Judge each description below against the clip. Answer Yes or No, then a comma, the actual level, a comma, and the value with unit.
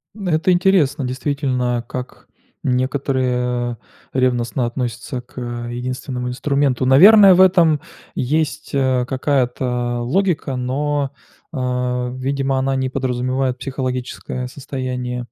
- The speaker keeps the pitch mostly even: Yes, narrow, 2.2 semitones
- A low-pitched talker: Yes, low, 130 Hz